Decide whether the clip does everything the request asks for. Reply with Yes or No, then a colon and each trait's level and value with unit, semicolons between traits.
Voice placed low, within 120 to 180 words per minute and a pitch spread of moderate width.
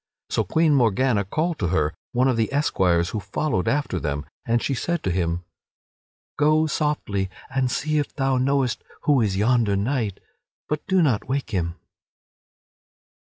No: low, 125 Hz; average, 160 wpm; wide, 7.2 semitones